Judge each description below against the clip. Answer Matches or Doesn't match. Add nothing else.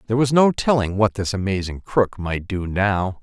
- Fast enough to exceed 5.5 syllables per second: Doesn't match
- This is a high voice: Doesn't match